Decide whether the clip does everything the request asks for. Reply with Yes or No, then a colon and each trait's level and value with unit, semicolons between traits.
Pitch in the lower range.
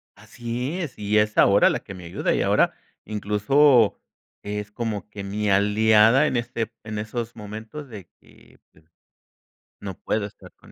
Yes: low, 105 Hz